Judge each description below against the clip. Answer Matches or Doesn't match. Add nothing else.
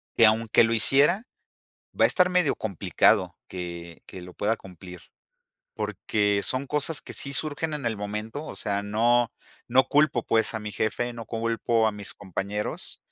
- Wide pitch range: Doesn't match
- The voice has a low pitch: Matches